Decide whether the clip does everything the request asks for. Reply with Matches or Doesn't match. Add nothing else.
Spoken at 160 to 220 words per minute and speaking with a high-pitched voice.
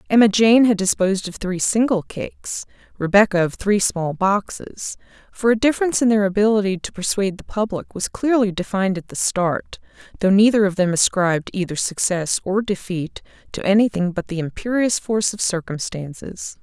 Matches